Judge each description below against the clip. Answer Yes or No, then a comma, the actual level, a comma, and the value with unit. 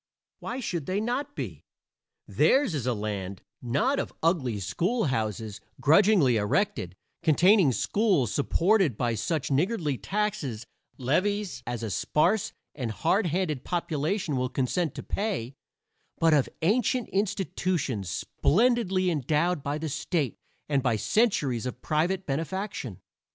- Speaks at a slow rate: Yes, slow, 125 wpm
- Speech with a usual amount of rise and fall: No, wide, 7.8 semitones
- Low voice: No, medium, 160 Hz